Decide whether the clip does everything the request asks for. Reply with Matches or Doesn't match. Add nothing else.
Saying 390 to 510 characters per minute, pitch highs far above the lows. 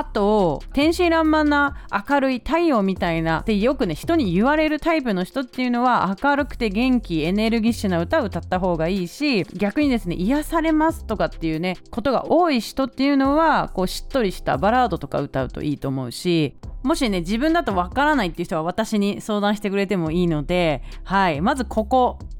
Matches